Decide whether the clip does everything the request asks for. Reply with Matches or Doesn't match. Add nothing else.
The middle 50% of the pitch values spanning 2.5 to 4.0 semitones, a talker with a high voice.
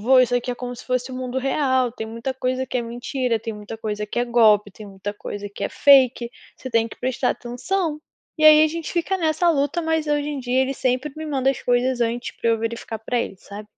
Matches